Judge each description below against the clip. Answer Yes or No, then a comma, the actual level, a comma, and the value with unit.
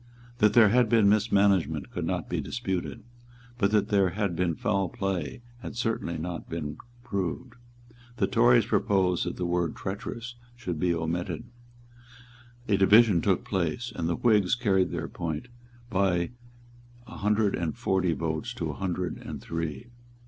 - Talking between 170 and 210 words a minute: No, average, 155 wpm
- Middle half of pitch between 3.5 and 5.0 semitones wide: Yes, average, 3.9 semitones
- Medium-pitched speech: No, very low, 95 Hz